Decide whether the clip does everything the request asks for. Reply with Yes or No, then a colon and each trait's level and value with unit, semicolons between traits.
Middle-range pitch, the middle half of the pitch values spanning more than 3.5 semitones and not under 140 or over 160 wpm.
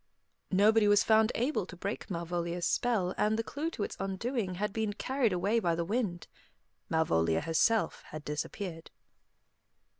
No: high, 200 Hz; average, 4.3 semitones; average, 150 wpm